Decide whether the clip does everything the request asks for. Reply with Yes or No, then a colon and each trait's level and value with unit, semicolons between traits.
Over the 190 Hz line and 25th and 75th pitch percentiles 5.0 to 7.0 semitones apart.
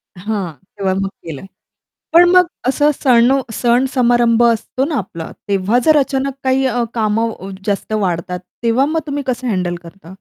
Yes: high, 235 Hz; average, 5.3 semitones